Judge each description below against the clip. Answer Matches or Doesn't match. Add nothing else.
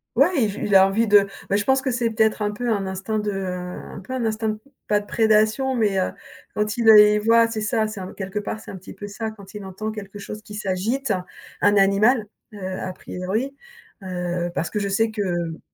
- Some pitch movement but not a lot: Doesn't match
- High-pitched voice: Matches